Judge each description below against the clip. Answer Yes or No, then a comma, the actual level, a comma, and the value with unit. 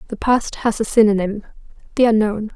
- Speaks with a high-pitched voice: Yes, high, 215 Hz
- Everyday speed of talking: Yes, average, 165 wpm